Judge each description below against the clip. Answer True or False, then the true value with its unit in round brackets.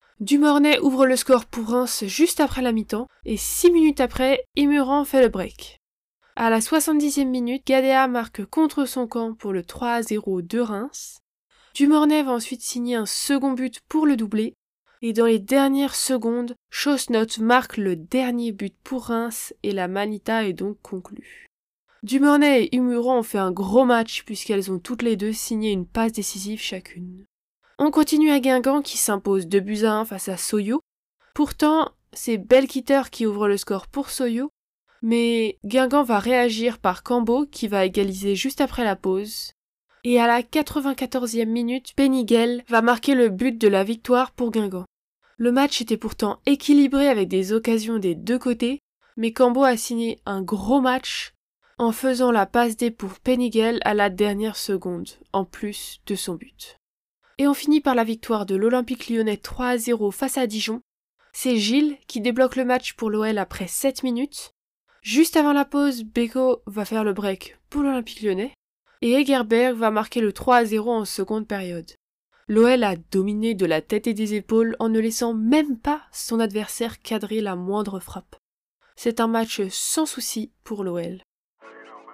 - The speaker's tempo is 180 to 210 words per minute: False (170 wpm)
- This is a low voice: False (235 Hz)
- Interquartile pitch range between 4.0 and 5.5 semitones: False (3.6 semitones)